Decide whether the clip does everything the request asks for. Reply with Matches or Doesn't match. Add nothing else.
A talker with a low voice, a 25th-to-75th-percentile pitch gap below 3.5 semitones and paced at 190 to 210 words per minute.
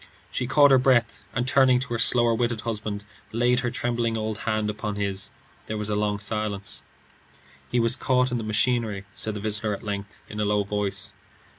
Matches